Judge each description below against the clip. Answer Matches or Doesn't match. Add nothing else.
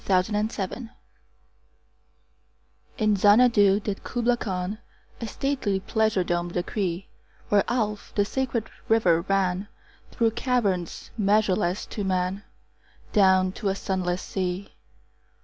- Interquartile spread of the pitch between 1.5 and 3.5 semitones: Matches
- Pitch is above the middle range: Matches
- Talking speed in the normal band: Doesn't match